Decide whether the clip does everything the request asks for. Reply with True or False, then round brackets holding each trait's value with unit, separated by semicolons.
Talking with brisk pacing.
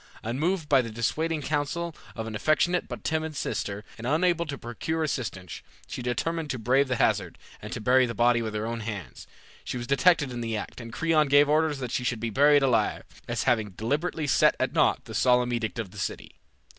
True (210 wpm)